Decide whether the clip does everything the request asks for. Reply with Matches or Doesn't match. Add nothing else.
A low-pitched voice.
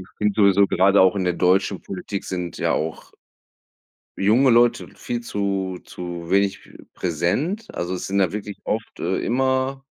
Matches